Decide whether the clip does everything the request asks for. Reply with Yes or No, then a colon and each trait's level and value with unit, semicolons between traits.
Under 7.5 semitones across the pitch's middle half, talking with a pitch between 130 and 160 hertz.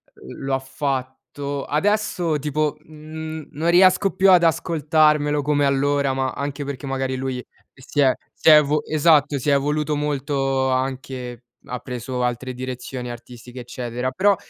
Yes: average, 2.7 semitones; medium, 140 Hz